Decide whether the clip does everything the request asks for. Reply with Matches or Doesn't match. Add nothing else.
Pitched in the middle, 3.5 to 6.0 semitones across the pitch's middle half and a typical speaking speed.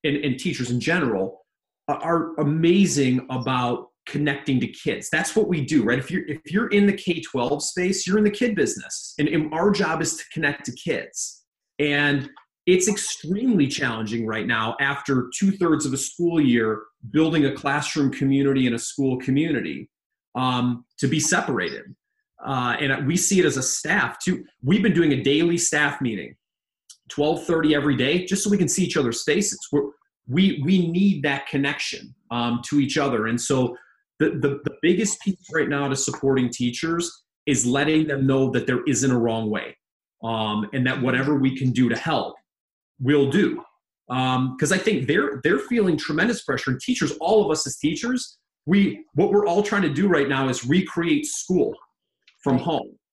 Matches